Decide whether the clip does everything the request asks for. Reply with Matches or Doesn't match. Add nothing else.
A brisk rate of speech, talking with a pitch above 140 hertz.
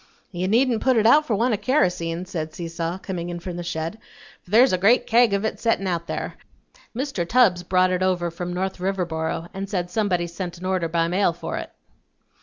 Matches